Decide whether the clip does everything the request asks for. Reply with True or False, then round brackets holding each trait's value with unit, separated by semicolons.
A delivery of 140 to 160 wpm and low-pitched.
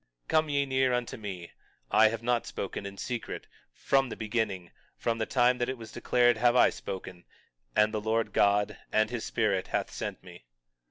False (195 wpm; 115 Hz)